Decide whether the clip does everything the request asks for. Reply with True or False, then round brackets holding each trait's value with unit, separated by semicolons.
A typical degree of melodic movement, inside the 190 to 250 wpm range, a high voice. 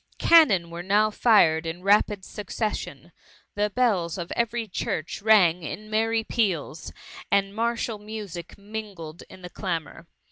False (4.1 semitones; 135 wpm; 200 Hz)